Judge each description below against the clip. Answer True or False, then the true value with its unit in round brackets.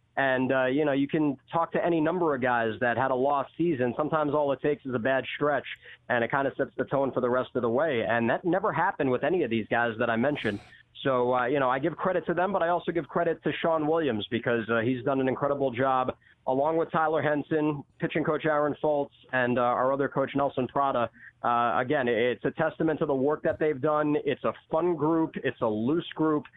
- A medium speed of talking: False (245 wpm)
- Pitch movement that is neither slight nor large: True (3.8 semitones)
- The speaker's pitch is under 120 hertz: False (140 Hz)